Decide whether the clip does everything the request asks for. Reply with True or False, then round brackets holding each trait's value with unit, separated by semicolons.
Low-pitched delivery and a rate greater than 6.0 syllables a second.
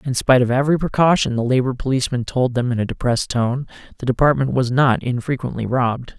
True (130 Hz; 6.5 syllables/s)